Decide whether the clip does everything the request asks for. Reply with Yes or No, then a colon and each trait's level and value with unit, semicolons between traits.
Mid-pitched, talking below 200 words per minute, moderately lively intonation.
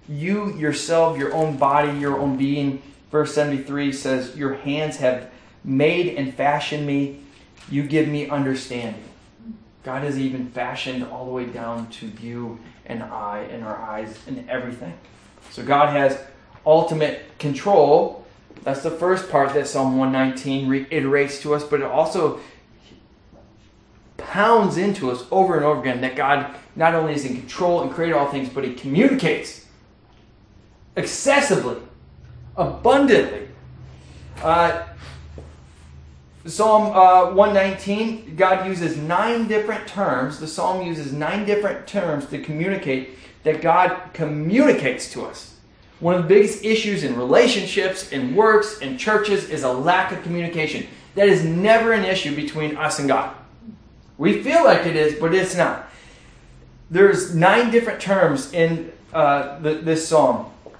No: medium, 150 Hz; average, 140 wpm; wide, 5.7 semitones